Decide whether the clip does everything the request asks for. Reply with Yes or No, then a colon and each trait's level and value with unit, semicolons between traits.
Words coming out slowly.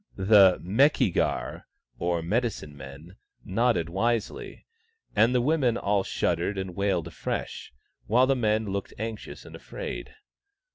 Yes: slow, 130 wpm